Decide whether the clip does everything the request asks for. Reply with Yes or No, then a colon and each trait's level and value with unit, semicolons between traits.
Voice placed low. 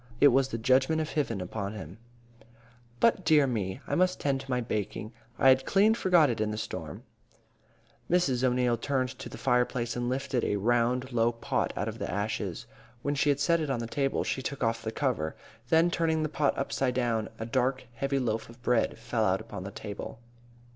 Yes: low, 125 Hz